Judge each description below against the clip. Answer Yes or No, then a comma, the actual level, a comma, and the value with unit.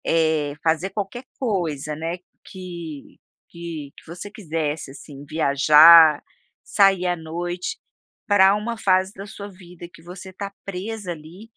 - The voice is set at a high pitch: No, medium, 175 Hz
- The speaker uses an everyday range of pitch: Yes, average, 3.6 semitones